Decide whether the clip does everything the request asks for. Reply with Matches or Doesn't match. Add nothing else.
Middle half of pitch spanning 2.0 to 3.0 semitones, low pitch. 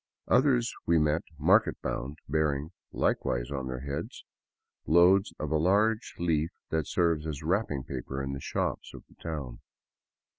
Doesn't match